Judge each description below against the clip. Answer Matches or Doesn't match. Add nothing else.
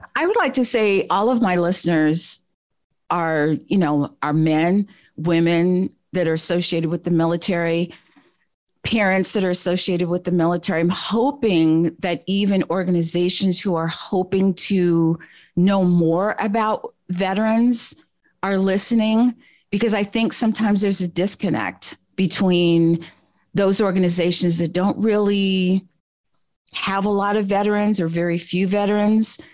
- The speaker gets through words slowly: Matches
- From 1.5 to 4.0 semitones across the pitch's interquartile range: Matches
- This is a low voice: Doesn't match